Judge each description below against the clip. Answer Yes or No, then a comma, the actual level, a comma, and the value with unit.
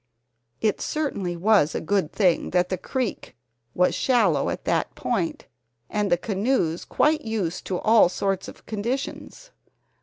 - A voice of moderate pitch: No, high, 205 Hz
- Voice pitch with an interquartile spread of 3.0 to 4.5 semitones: No, average, 4.9 semitones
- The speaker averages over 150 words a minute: No, average, 145 wpm